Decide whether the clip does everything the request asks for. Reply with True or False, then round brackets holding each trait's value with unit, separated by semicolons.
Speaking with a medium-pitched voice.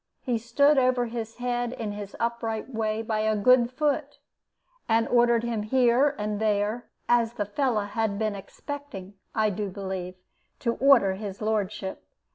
False (225 Hz)